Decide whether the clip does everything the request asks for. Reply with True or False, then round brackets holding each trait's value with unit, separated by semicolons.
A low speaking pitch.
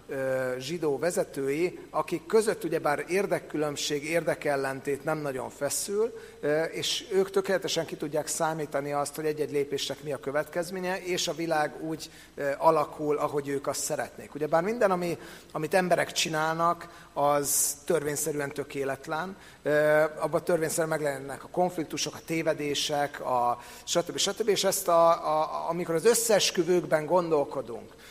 False (155 Hz)